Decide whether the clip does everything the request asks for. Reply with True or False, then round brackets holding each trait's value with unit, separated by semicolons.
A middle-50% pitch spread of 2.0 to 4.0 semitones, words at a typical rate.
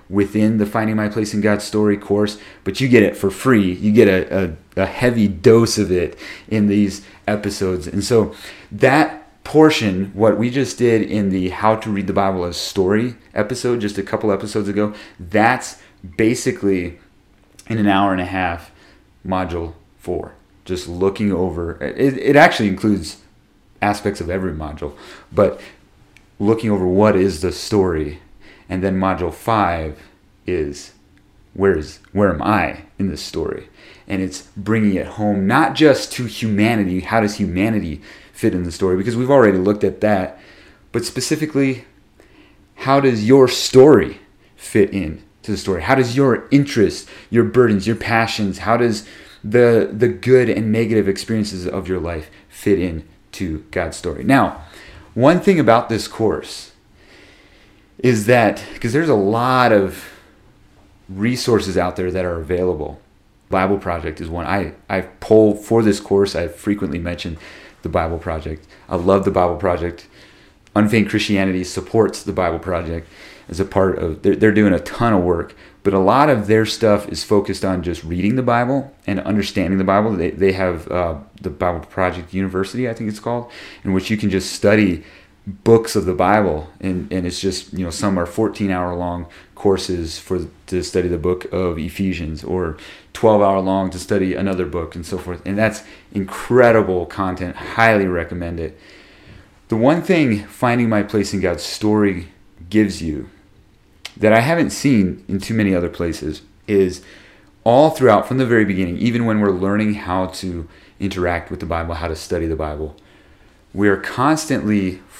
True (3.0 semitones; 170 wpm)